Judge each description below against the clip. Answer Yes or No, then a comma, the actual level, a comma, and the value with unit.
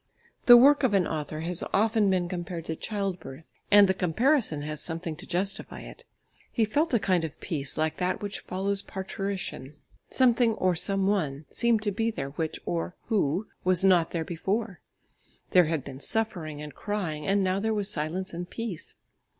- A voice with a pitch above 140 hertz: Yes, medium, 185 Hz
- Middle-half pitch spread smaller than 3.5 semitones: No, average, 4.3 semitones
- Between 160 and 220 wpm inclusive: Yes, average, 180 wpm